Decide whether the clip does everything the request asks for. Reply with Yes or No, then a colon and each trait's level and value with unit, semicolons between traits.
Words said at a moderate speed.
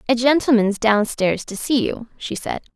Yes: average, 175 wpm